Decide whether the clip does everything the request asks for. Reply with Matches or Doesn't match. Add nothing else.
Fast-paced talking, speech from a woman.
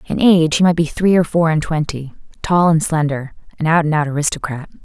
Matches